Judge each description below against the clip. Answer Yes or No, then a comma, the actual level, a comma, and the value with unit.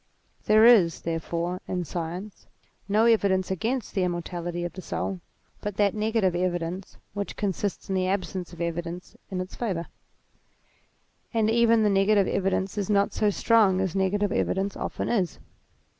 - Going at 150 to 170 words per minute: Yes, average, 155 wpm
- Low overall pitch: No, high, 190 Hz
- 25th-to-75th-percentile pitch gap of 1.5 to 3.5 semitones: Yes, average, 2.8 semitones